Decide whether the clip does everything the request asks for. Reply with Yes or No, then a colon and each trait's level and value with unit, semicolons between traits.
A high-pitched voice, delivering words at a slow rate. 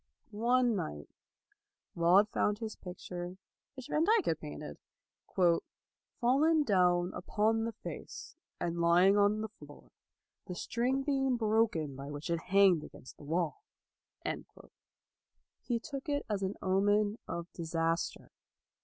Yes: high, 200 Hz; slow, 125 wpm